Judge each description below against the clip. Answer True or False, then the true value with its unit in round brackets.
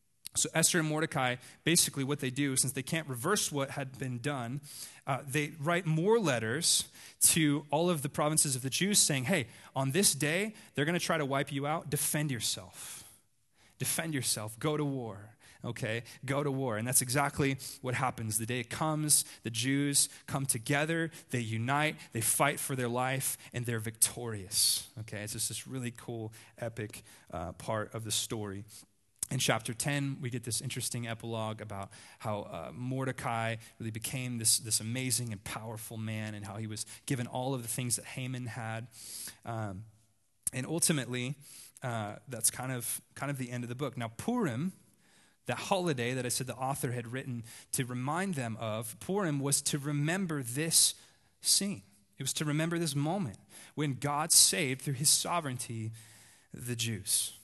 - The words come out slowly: False (175 wpm)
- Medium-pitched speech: False (130 Hz)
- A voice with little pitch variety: False (4.5 semitones)